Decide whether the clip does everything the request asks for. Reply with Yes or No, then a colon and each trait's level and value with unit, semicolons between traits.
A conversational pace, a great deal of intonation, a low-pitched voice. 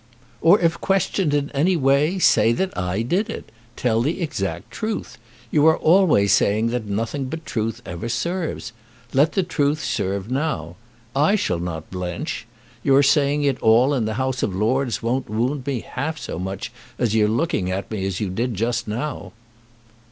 Yes: average, 175 wpm; wide, 6.1 semitones; low, 125 Hz